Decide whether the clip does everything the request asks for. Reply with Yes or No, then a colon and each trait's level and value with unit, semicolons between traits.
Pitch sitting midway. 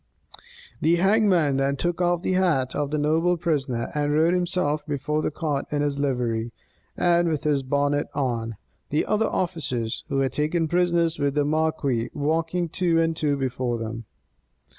Yes: medium, 150 Hz